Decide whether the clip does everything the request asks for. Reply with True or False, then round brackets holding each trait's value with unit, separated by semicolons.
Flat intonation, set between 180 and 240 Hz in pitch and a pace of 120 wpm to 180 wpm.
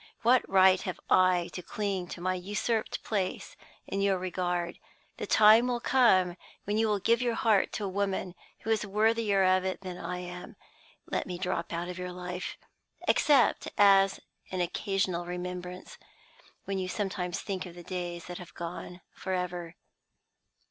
True (2.3 semitones; 185 Hz; 165 wpm)